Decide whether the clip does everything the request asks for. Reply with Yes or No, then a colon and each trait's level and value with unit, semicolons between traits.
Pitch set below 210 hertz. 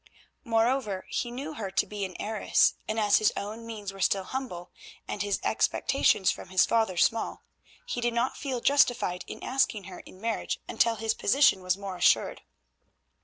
No: high, 215 Hz